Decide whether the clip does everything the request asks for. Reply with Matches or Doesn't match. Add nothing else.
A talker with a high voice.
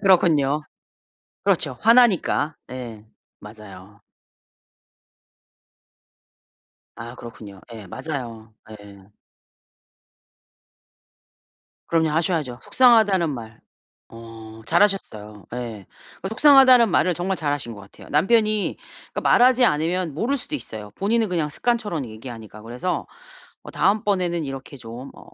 Doesn't match